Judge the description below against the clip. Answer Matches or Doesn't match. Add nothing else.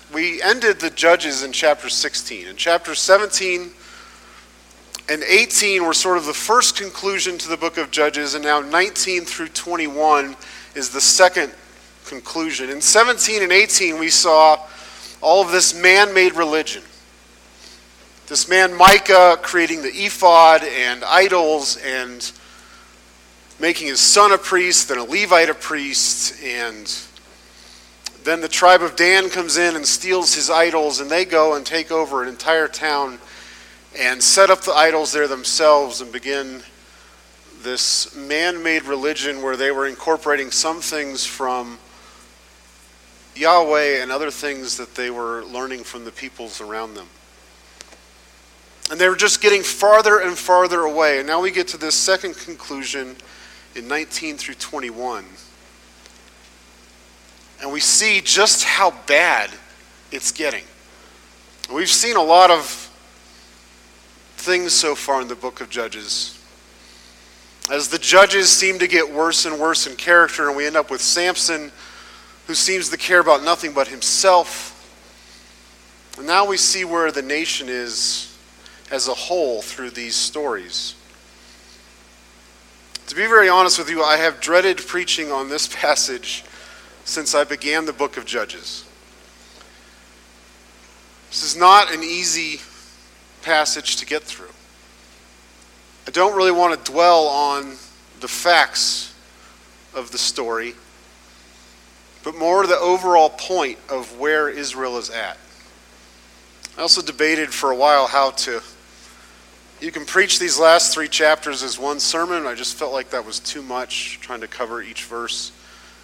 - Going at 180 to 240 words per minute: Doesn't match